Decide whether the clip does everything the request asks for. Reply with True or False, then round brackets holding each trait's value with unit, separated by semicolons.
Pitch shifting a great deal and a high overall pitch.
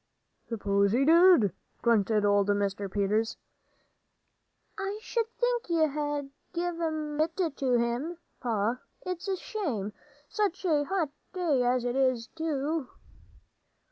True (6.9 semitones; 285 Hz)